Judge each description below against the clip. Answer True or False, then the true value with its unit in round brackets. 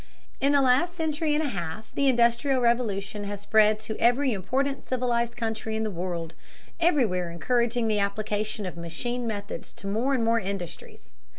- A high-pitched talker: True (225 Hz)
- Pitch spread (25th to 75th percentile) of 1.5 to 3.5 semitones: False (4.0 semitones)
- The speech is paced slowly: False (170 wpm)